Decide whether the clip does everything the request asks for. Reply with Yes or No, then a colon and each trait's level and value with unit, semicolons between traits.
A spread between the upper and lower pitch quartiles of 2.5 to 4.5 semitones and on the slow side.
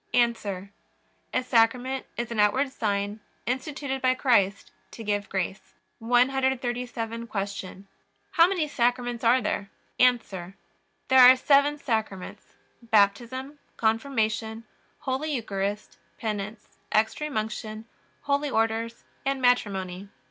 Yes: average, 3.6 semitones; slow, 105 wpm